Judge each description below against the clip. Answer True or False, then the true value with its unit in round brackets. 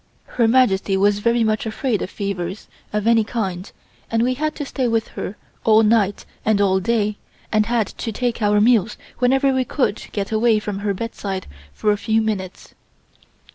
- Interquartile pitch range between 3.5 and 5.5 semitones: False (2.4 semitones)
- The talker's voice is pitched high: True (220 Hz)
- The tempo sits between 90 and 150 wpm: False (180 wpm)